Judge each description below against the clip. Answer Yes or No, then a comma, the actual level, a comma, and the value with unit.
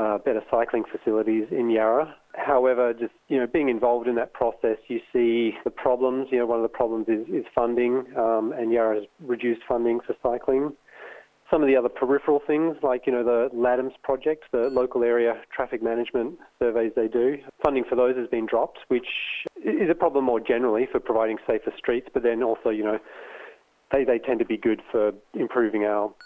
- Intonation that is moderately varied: No, narrow, 2.1 semitones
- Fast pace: No, average, 195 wpm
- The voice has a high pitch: No, low, 120 Hz